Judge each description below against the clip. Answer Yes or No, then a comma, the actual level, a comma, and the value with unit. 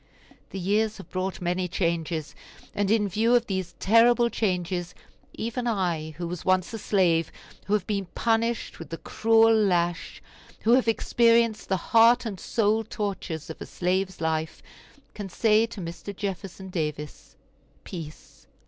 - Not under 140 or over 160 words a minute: Yes, average, 150 wpm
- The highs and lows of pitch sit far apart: No, average, 4.3 semitones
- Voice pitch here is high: Yes, high, 195 Hz